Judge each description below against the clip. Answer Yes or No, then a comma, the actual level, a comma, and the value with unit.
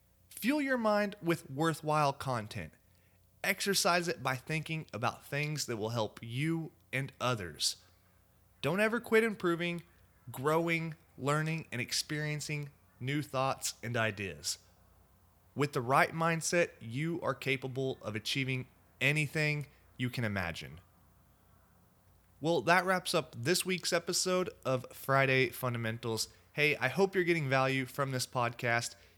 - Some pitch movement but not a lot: No, wide, 7.2 semitones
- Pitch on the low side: Yes, low, 130 Hz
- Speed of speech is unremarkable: No, slow, 130 wpm